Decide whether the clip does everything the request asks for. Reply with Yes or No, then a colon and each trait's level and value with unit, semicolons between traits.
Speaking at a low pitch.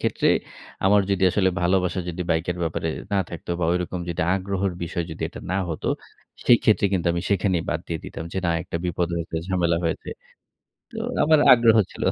Yes: very low, 90 Hz